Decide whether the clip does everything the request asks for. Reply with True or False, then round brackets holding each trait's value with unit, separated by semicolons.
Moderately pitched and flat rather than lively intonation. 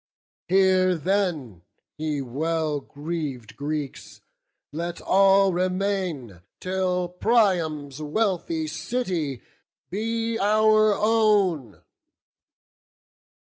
False (180 Hz; 4.7 semitones)